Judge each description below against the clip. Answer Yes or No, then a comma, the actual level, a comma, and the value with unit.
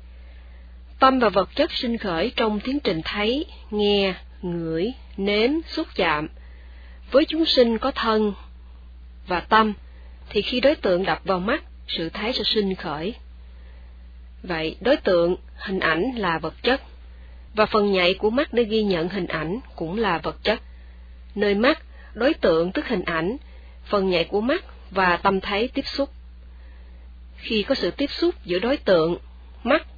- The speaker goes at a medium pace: No, slow, 160 wpm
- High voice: No, medium, 180 Hz